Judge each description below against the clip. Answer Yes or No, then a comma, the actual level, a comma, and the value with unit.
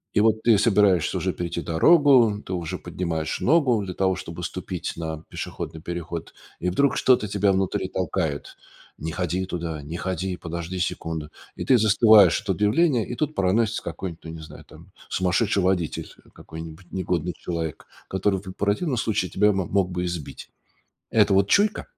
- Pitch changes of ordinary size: Yes, average, 3.7 semitones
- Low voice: Yes, very low, 95 Hz